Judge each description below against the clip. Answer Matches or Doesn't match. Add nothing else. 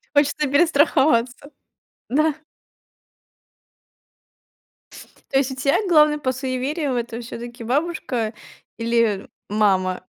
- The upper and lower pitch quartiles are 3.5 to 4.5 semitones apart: Matches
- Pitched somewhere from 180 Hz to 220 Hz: Doesn't match